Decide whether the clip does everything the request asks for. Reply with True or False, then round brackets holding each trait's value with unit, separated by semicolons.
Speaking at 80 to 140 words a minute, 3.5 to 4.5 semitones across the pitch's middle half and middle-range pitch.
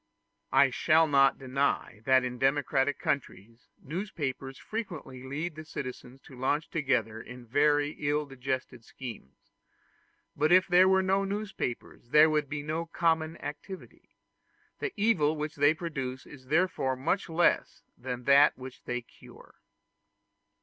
True (135 wpm; 3.8 semitones; 145 Hz)